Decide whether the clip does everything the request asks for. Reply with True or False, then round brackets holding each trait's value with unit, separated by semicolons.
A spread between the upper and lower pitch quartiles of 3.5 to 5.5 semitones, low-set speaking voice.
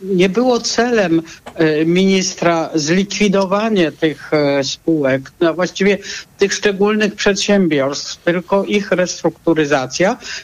False (3.8 semitones; 180 Hz)